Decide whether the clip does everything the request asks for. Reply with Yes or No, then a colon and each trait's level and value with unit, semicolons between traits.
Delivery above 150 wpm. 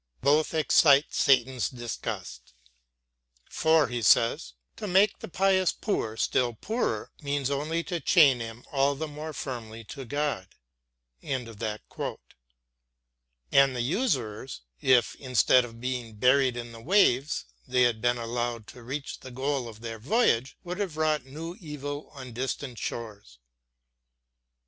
No: slow, 135 wpm